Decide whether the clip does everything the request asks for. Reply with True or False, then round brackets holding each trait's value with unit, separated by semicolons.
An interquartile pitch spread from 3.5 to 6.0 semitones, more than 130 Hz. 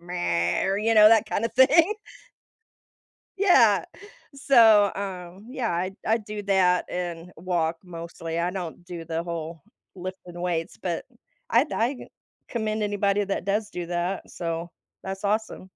True (3.8 semitones; 190 Hz)